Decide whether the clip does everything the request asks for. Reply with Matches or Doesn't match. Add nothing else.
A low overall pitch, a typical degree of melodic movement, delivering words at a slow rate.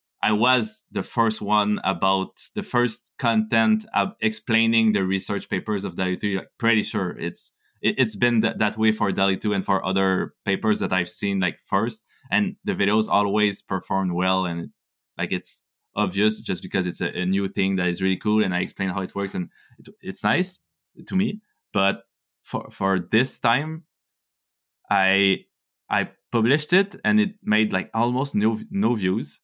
Doesn't match